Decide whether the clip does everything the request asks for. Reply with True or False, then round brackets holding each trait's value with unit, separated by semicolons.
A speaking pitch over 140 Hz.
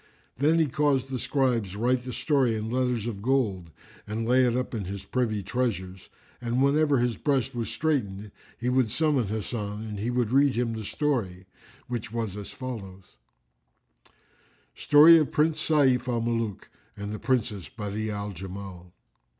False (120 Hz)